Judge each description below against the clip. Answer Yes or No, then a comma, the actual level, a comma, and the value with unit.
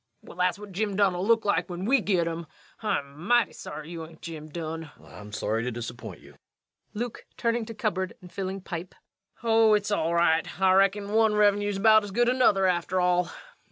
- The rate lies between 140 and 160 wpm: No, average, 200 wpm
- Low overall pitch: No, high, 190 Hz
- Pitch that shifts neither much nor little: Yes, average, 3.9 semitones